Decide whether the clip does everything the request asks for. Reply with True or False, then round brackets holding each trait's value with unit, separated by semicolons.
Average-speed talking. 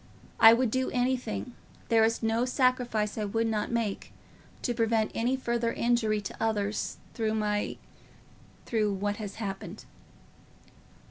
False (130 wpm)